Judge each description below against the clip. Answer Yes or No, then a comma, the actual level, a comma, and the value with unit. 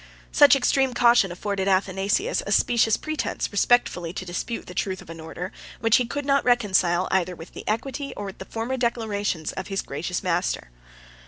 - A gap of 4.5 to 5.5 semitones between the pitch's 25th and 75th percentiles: Yes, average, 5.1 semitones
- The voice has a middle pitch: No, high, 205 Hz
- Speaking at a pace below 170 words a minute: No, average, 180 wpm